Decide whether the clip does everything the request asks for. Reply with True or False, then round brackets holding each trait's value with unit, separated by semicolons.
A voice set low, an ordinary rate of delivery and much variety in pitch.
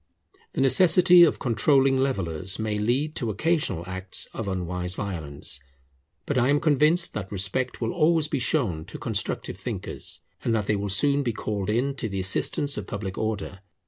True (110 Hz; 175 wpm; 6.5 semitones)